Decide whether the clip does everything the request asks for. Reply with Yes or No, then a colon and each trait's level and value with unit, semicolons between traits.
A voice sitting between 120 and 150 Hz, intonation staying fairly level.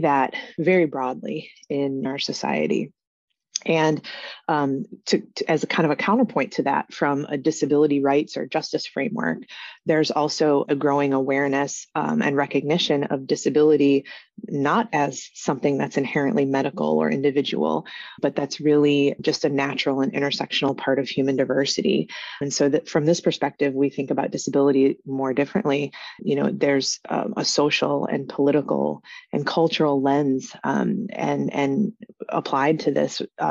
Yes: medium, 140 Hz; narrow, 1.8 semitones